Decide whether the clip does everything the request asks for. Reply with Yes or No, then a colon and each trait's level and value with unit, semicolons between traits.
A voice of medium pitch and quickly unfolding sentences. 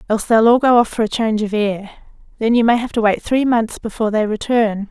No: high, 225 Hz; fast, 255 wpm